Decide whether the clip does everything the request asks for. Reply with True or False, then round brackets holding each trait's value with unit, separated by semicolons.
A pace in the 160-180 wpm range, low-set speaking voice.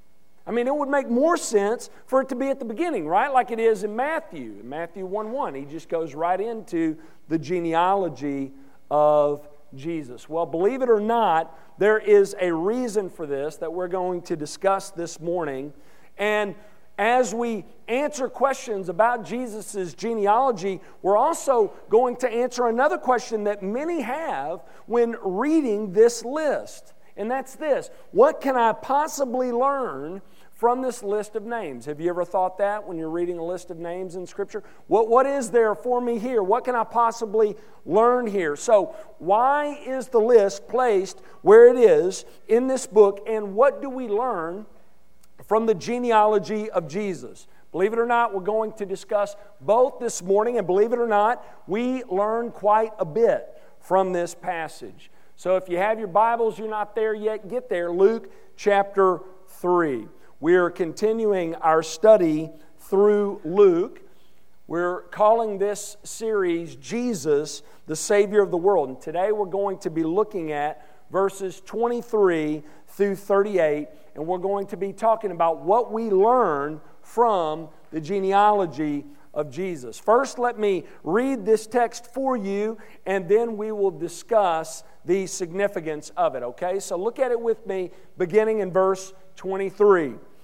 False (165 wpm; 205 Hz)